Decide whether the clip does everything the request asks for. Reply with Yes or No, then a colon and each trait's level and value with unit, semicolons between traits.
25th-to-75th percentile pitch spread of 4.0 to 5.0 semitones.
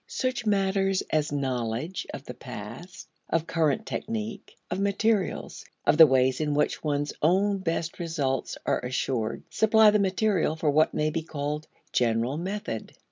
No: wide, 5.5 semitones